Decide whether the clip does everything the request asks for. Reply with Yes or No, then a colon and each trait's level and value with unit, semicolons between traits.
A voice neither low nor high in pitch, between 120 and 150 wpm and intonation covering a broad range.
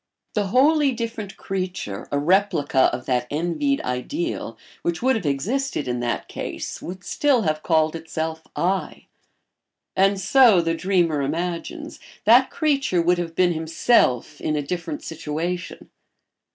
Yes: medium, 175 Hz; average, 140 wpm; wide, 6.3 semitones